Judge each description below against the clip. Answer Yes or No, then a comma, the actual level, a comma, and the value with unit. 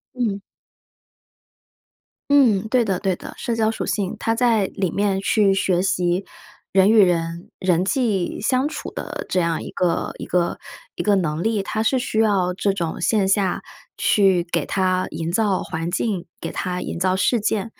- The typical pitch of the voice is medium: No, high, 195 Hz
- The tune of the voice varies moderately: Yes, average, 3.4 semitones